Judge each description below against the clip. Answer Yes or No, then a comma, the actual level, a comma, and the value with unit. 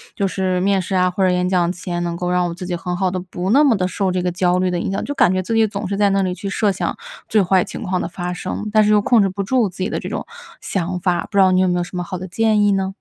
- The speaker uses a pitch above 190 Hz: No, medium, 185 Hz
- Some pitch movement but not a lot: No, narrow, 1.9 semitones